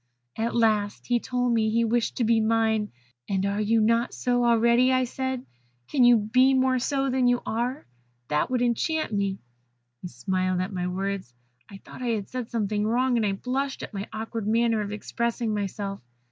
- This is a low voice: No, high, 225 Hz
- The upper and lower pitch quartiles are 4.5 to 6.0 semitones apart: No, average, 3.2 semitones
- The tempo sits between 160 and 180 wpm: No, average, 195 wpm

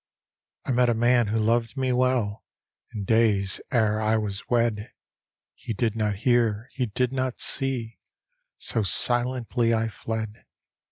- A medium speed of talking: Yes, average, 145 wpm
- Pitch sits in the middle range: No, low, 115 Hz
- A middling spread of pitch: No, narrow, 2.3 semitones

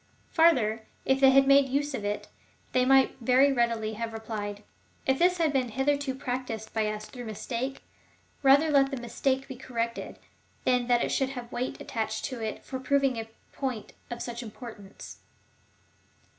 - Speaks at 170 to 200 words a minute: Yes, average, 175 wpm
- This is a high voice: Yes, very high, 250 Hz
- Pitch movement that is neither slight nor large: Yes, average, 3.2 semitones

